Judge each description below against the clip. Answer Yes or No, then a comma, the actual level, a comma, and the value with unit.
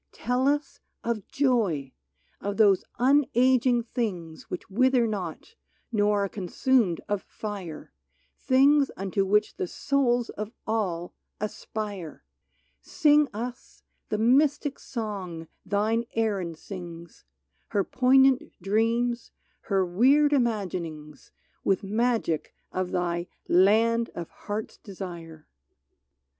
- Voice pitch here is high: Yes, high, 210 Hz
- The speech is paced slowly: Yes, slow, 110 wpm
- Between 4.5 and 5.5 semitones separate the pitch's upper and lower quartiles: Yes, average, 5.1 semitones